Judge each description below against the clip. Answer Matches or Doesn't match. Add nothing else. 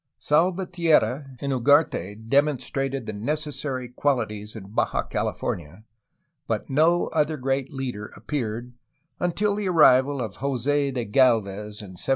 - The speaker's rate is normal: Doesn't match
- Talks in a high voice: Doesn't match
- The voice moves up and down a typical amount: Matches